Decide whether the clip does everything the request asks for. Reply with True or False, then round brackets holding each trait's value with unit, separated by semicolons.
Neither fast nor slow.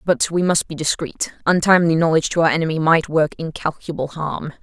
True (180 wpm)